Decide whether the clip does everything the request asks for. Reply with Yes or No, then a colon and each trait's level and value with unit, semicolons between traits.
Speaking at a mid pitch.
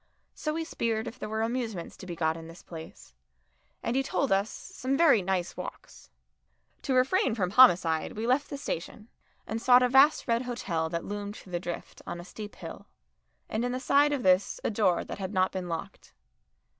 No: high, 220 Hz